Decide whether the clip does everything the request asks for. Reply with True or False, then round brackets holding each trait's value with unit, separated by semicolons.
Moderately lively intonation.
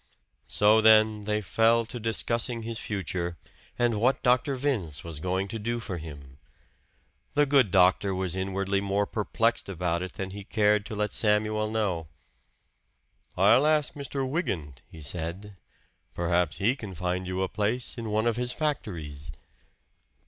True (4.2 semitones)